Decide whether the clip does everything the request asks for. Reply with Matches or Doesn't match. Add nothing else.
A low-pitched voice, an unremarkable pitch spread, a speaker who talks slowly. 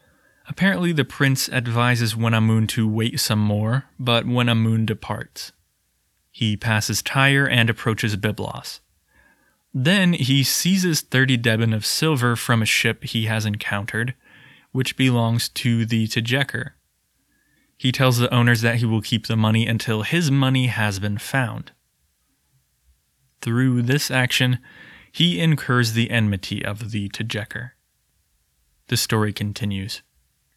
Matches